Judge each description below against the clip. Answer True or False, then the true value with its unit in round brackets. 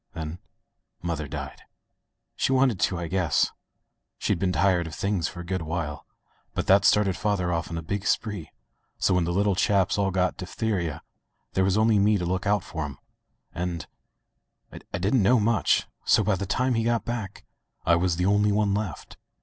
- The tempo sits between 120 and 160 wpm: False (200 wpm)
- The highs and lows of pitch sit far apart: False (3.2 semitones)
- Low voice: True (95 Hz)